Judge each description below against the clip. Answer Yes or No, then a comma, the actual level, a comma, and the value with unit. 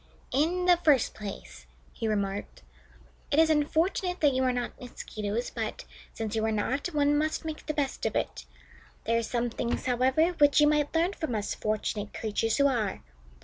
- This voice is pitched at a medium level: No, very high, 260 Hz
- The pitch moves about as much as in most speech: No, wide, 5.7 semitones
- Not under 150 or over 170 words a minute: No, average, 185 wpm